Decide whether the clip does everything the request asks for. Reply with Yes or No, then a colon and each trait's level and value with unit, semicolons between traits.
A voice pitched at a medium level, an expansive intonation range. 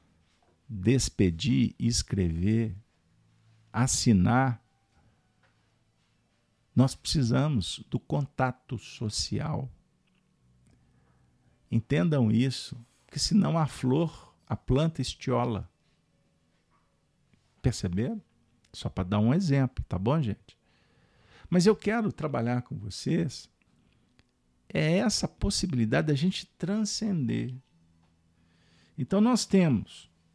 No: low, 120 Hz; wide, 6.8 semitones